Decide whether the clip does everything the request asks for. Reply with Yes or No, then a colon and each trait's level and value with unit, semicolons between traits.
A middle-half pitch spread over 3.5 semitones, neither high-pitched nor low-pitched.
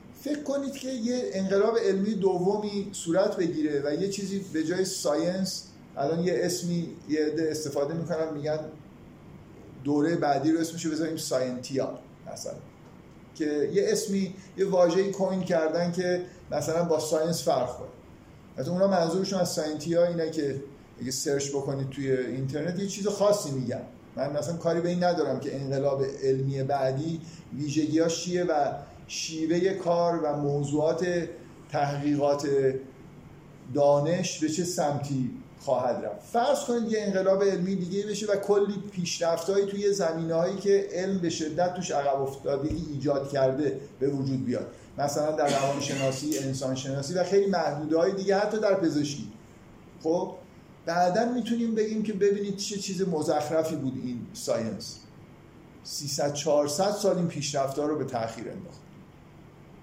Yes: average, 4.8 semitones; medium, 165 Hz